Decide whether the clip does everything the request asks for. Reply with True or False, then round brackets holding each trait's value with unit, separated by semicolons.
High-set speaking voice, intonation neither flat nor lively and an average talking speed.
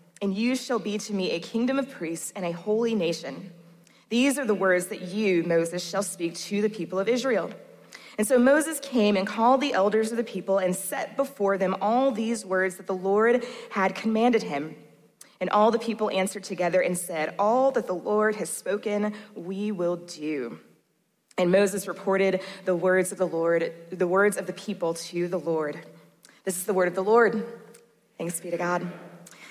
True (195 Hz; 3.5 semitones; 195 wpm)